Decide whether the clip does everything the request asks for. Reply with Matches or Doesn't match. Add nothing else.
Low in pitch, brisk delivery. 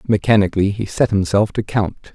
Doesn't match